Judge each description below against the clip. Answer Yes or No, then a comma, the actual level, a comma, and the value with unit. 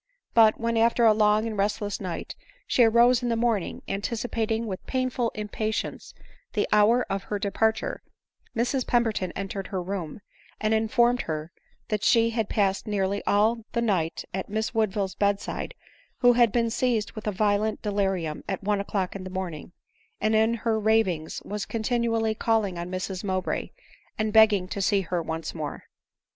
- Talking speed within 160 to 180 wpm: Yes, average, 170 wpm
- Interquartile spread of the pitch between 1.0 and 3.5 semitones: Yes, narrow, 2.6 semitones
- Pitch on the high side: Yes, high, 210 Hz